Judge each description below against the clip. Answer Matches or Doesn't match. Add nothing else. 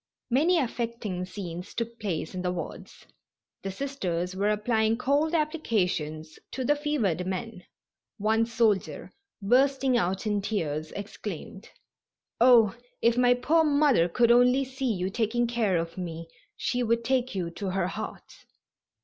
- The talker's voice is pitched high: Matches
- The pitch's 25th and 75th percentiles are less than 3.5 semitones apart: Doesn't match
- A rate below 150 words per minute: Matches